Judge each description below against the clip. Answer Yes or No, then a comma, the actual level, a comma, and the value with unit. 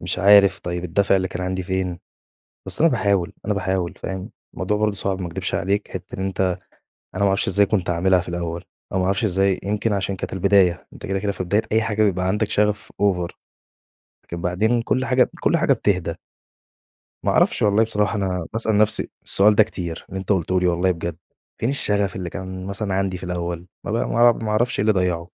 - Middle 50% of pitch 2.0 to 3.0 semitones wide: Yes, narrow, 2.4 semitones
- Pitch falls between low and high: No, very low, 95 Hz